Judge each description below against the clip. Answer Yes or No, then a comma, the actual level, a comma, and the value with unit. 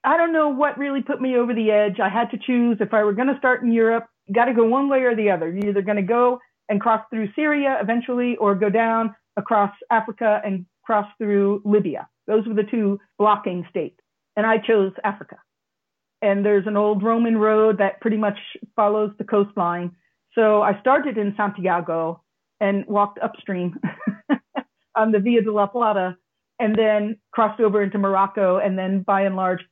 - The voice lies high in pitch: Yes, high, 215 Hz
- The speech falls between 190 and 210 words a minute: Yes, average, 195 wpm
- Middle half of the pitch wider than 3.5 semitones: No, narrow, 2.4 semitones